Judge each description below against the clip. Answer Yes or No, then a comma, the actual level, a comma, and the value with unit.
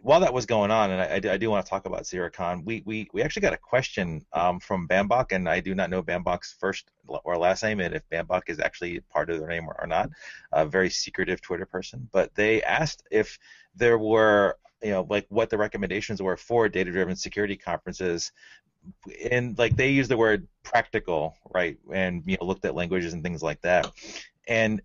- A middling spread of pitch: Yes, average, 3.7 semitones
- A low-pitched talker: Yes, very low, 95 Hz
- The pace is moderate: No, fast, 210 wpm